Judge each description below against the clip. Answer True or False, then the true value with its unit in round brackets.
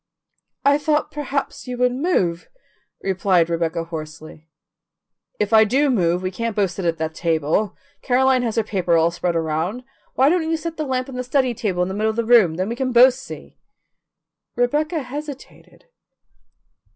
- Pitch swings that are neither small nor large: False (7.3 semitones)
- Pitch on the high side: True (225 Hz)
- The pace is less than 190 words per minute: True (175 wpm)